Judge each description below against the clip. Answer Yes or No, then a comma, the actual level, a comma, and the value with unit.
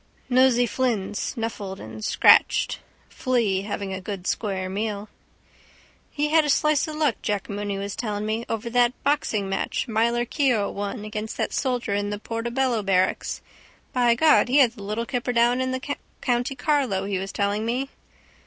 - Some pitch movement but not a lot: Yes, average, 3.8 semitones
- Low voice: No, high, 230 Hz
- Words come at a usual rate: Yes, average, 170 wpm